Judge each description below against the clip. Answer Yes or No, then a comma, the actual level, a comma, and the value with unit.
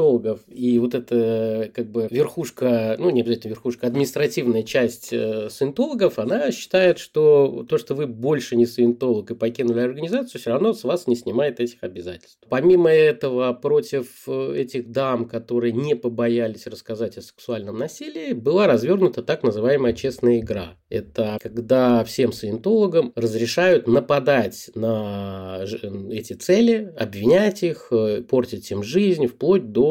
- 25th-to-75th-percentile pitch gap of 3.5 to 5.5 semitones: Yes, average, 4.7 semitones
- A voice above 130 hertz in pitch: No, low, 120 Hz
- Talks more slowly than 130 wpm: No, average, 135 wpm